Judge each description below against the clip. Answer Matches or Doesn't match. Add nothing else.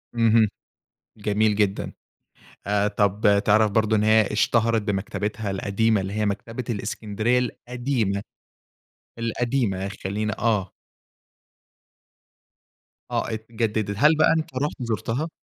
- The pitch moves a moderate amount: Doesn't match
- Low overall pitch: Matches